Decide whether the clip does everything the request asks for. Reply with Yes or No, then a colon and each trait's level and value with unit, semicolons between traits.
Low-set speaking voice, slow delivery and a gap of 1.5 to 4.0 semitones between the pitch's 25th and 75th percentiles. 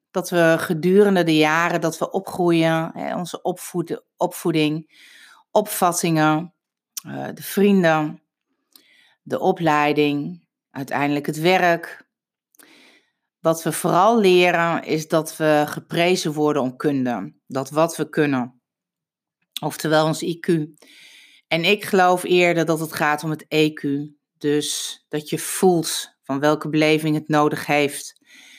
No: medium, 160 Hz; slow, 120 wpm; average, 2.7 semitones